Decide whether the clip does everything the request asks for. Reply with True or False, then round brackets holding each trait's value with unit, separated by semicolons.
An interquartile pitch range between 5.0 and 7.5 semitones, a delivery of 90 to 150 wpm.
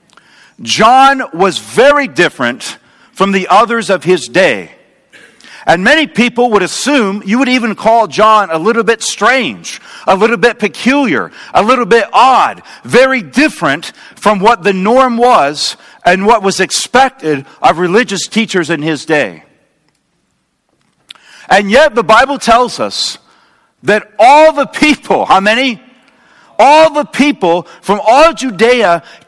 True (5.3 semitones; 135 wpm)